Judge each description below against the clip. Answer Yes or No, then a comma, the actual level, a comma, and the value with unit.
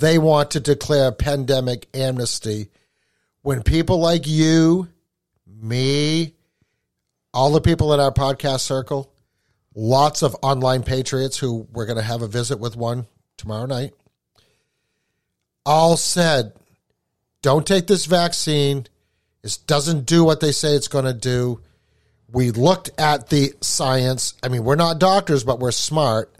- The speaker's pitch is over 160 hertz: No, low, 135 Hz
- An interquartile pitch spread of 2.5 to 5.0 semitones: Yes, average, 4.4 semitones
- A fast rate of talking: No, average, 145 wpm